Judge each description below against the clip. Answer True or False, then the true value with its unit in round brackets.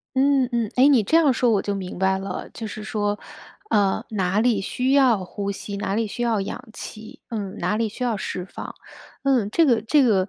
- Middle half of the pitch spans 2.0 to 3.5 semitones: False (3.9 semitones)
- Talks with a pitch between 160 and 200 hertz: False (215 Hz)